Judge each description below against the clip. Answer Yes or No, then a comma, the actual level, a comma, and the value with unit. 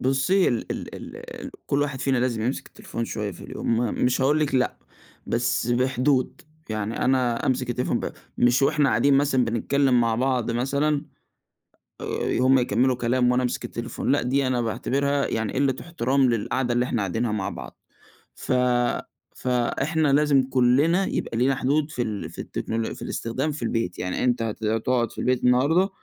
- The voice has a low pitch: Yes, low, 125 Hz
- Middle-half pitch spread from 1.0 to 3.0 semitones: Yes, average, 2.7 semitones